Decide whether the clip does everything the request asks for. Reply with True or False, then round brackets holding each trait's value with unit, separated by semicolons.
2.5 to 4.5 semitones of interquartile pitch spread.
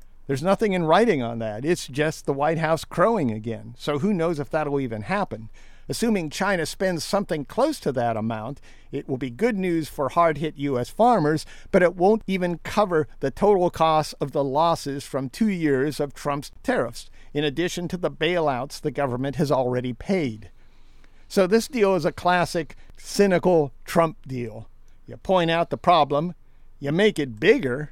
False (5.2 semitones)